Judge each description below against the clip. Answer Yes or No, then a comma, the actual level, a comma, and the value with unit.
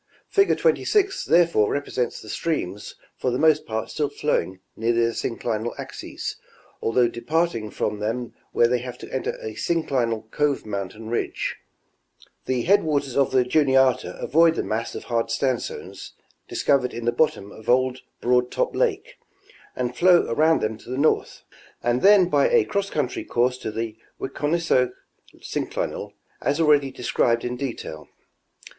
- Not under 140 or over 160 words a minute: Yes, average, 155 wpm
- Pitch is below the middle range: Yes, low, 125 Hz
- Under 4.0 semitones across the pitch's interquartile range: No, average, 4.7 semitones